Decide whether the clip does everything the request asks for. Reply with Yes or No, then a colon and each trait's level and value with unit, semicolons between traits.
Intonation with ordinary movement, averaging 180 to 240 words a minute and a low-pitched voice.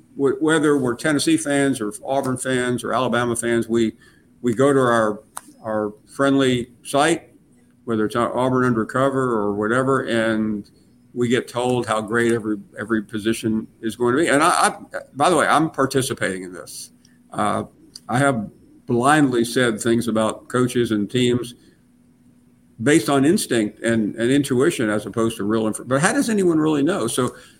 No: average, 3.3 semitones; average, 165 wpm; low, 120 Hz